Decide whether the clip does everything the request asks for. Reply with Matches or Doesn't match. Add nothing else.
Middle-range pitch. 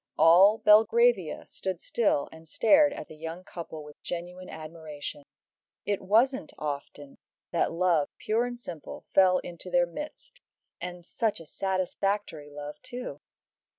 Matches